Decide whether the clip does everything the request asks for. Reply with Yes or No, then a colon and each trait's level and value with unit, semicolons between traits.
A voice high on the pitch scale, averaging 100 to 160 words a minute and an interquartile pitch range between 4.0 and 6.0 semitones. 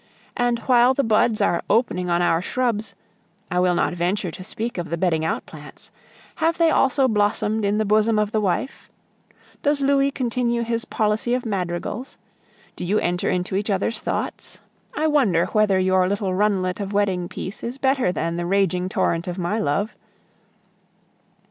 No: high, 205 Hz; average, 175 wpm; average, 4.7 semitones